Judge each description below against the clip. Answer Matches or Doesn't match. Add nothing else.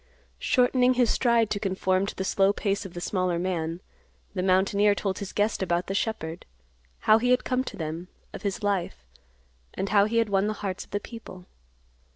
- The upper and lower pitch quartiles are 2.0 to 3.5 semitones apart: Matches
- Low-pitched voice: Doesn't match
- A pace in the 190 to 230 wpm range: Matches